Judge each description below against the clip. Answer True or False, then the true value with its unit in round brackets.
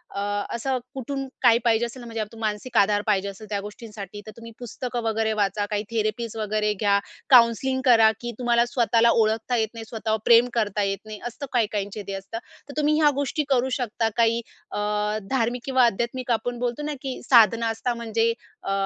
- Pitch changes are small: True (2.3 semitones)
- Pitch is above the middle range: True (230 Hz)